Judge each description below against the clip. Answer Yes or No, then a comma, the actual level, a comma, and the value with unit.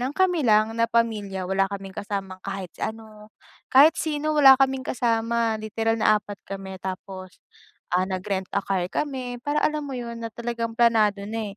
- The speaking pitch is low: No, high, 220 Hz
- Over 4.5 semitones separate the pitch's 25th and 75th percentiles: No, average, 3.7 semitones